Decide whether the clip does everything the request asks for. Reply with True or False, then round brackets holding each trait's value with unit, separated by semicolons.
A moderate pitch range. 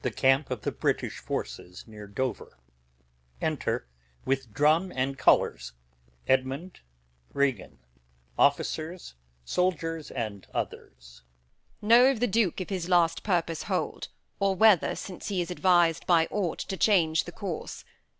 False (5.9 semitones)